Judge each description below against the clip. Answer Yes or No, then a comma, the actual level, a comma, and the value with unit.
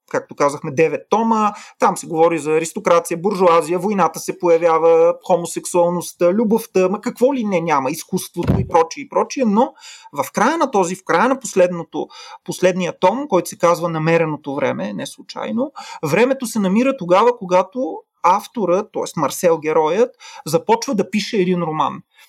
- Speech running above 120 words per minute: Yes, average, 155 wpm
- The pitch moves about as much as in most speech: No, wide, 6.0 semitones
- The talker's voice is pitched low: No, medium, 185 Hz